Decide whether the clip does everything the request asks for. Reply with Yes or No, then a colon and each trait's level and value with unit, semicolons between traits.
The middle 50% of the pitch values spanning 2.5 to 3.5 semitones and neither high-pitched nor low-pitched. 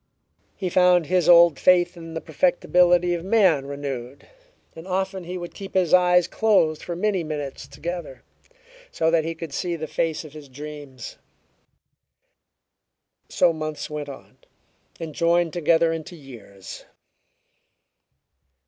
Yes: average, 2.8 semitones; medium, 165 Hz